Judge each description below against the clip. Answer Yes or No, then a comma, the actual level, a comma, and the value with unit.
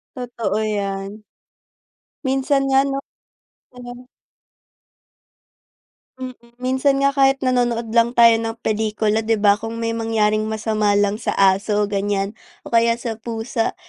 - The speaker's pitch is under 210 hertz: No, high, 225 Hz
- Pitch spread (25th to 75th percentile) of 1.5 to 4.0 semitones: Yes, average, 2.8 semitones